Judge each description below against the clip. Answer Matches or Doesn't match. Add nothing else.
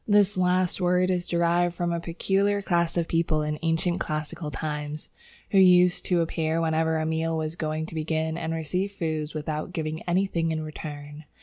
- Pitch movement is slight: Matches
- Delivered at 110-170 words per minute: Doesn't match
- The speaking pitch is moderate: Matches